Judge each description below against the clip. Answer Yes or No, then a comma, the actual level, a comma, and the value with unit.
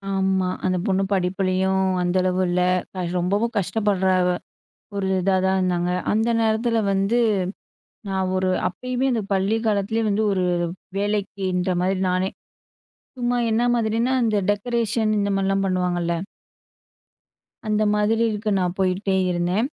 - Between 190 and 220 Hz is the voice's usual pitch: Yes, high, 195 Hz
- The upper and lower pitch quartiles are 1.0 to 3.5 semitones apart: Yes, average, 2.8 semitones